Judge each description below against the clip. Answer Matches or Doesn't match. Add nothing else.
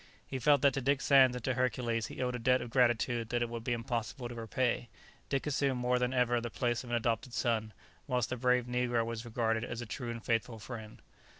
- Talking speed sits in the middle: Doesn't match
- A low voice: Matches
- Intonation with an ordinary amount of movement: Doesn't match